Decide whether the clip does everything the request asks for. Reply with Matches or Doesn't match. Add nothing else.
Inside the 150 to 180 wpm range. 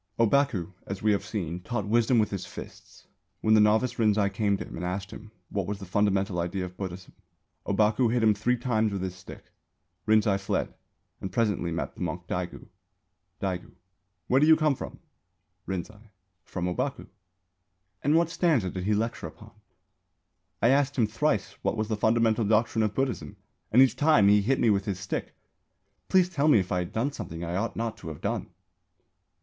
Doesn't match